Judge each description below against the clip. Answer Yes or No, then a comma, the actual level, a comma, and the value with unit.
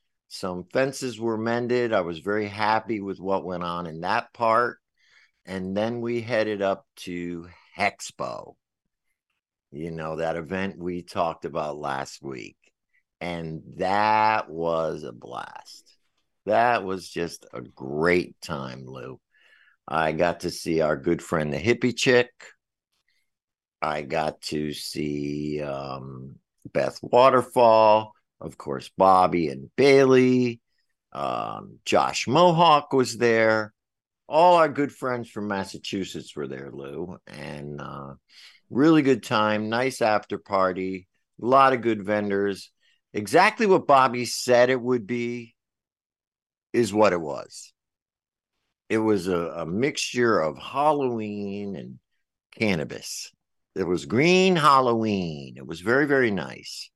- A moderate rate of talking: No, slow, 125 wpm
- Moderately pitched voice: No, low, 105 Hz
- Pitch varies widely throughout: Yes, wide, 6.0 semitones